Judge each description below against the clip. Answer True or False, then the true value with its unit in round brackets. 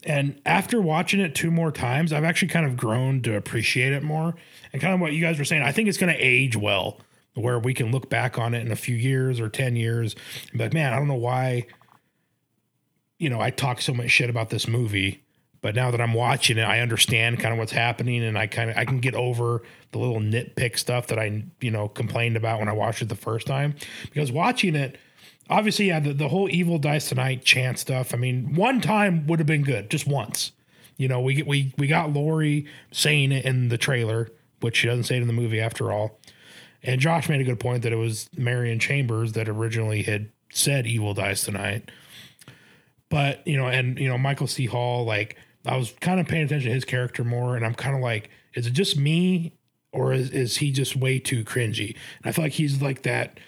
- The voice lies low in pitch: True (125 Hz)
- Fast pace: True (230 wpm)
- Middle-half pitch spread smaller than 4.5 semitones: True (4.0 semitones)